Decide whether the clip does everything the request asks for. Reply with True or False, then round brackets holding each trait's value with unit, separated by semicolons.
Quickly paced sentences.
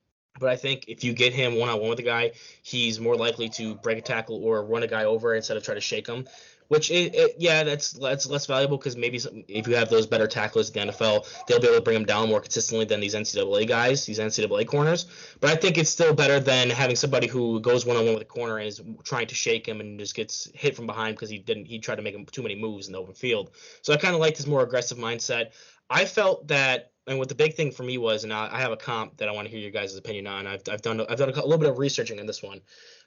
True (290 wpm)